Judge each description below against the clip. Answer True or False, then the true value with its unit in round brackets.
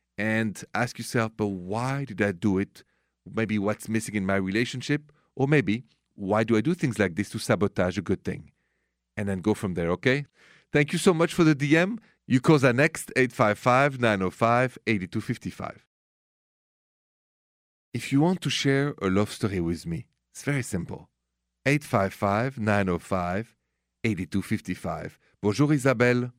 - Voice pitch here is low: True (110 Hz)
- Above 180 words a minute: False (145 wpm)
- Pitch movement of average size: False (5.7 semitones)